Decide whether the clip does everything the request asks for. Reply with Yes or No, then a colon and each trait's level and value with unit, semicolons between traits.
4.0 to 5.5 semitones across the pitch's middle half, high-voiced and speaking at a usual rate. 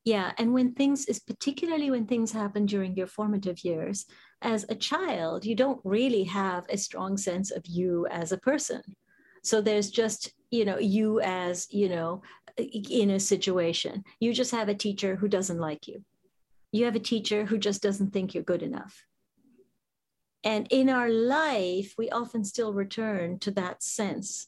No: average, 3.3 semitones; high, 210 Hz; average, 175 wpm